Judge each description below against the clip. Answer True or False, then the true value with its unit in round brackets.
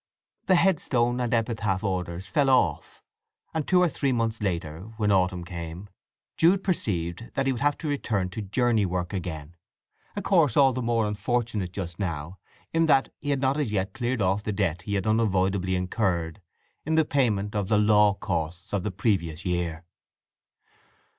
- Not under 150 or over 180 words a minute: True (175 wpm)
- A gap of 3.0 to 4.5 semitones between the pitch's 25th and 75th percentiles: False (5.2 semitones)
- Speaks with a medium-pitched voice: False (105 Hz)